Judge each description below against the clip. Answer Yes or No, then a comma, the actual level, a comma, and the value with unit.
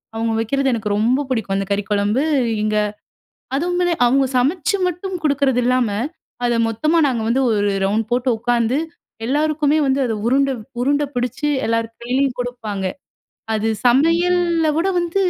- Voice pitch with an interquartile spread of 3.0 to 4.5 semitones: No, average, 4.9 semitones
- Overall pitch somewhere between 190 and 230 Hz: No, very high, 255 Hz